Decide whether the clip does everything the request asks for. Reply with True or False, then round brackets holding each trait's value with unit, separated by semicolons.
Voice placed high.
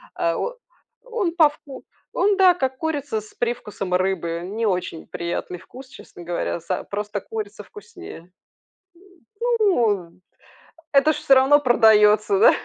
True (240 Hz)